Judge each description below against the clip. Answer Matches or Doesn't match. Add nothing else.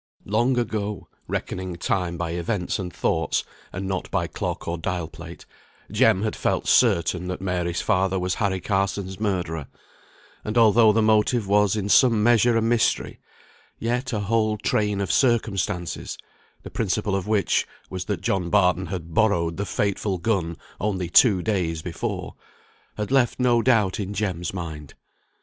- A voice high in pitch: Doesn't match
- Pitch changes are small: Doesn't match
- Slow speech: Doesn't match